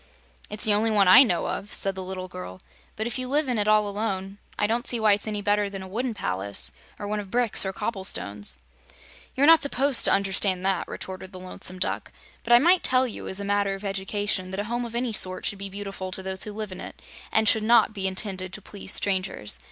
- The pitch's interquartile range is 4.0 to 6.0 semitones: No, narrow, 2.6 semitones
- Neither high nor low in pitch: No, high, 205 Hz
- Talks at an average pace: No, fast, 245 wpm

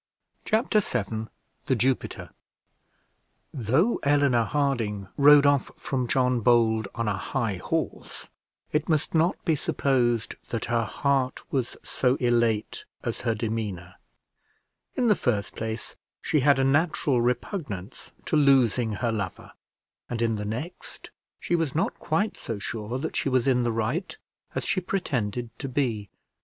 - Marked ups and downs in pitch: No, average, 4.2 semitones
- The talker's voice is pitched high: No, low, 125 Hz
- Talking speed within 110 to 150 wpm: Yes, average, 145 wpm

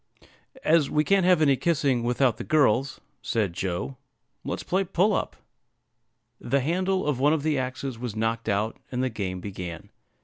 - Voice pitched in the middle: No, low, 130 Hz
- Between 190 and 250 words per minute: No, average, 170 wpm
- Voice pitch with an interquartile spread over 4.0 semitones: Yes, wide, 5.6 semitones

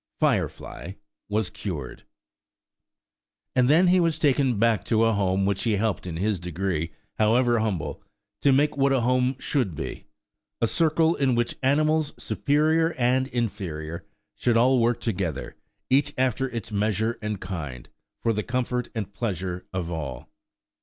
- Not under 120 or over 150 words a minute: Yes, average, 145 wpm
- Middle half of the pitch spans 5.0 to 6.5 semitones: Yes, wide, 5.4 semitones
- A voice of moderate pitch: No, low, 115 Hz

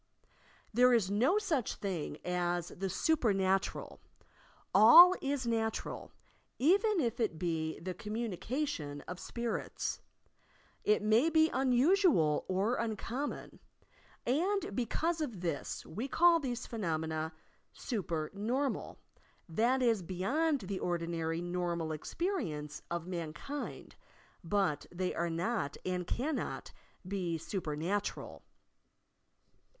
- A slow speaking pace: Yes, slow, 115 wpm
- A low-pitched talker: No, high, 205 Hz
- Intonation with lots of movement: Yes, wide, 7.3 semitones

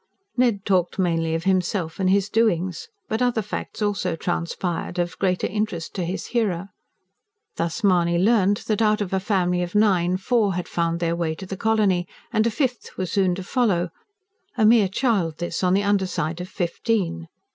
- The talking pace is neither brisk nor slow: Yes, average, 185 wpm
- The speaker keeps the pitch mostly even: No, average, 3.4 semitones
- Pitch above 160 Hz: Yes, high, 190 Hz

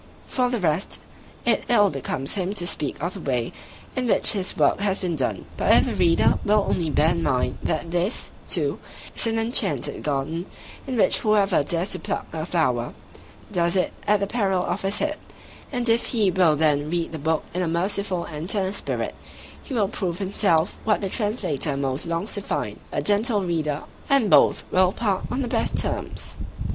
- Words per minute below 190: No, average, 195 wpm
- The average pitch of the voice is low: No, medium, 185 Hz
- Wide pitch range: No, average, 4.5 semitones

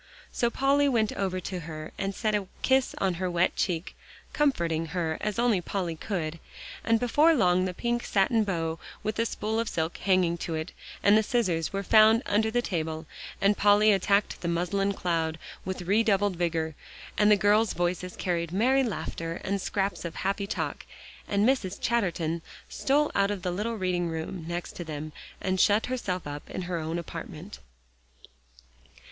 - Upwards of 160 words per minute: Yes, average, 175 wpm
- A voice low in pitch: No, high, 190 Hz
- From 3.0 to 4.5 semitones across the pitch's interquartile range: Yes, average, 4.1 semitones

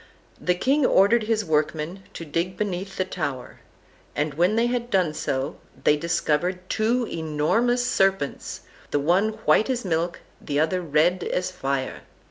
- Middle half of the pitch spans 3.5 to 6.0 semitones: Yes, wide, 5.6 semitones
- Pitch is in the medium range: Yes, medium, 180 Hz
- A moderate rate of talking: Yes, average, 150 wpm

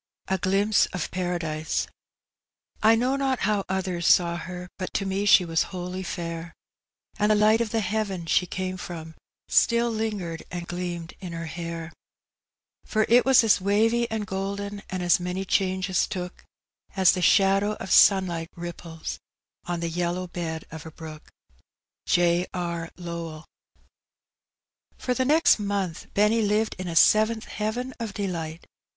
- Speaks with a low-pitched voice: No, medium, 185 Hz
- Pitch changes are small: No, average, 3.6 semitones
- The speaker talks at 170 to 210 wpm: No, average, 155 wpm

